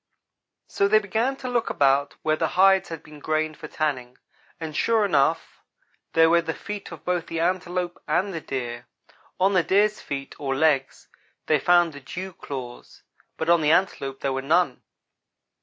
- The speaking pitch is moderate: Yes, medium, 165 Hz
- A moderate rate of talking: Yes, average, 175 wpm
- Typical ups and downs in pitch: Yes, average, 4.7 semitones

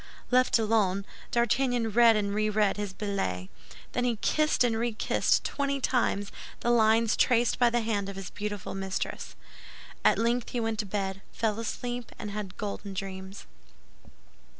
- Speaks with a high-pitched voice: Yes, high, 215 Hz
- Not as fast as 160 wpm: Yes, average, 150 wpm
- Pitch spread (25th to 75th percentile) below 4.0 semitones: Yes, average, 3.0 semitones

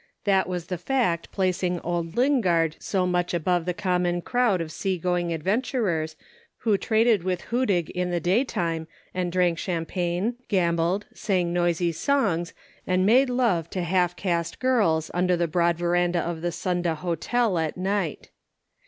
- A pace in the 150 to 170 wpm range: Yes, average, 155 wpm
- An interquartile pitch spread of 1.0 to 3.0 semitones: Yes, narrow, 2.4 semitones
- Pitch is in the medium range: Yes, medium, 180 Hz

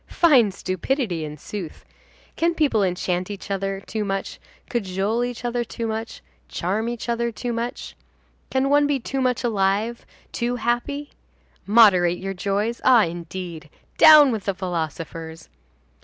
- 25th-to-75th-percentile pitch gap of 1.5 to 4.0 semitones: No, average, 4.5 semitones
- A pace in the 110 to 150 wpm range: Yes, average, 140 wpm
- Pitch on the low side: No, high, 215 Hz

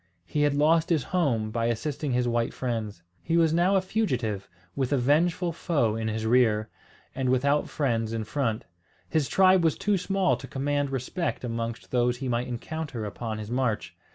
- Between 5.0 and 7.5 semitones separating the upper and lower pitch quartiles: Yes, wide, 5.6 semitones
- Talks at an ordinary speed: Yes, average, 180 wpm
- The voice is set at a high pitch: No, low, 130 Hz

